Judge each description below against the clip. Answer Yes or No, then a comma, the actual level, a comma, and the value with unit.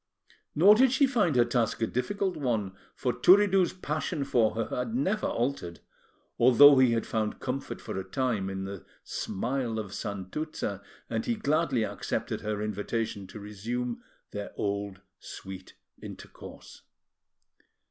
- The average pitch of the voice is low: Yes, low, 120 Hz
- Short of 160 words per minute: Yes, average, 140 wpm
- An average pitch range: No, wide, 6.1 semitones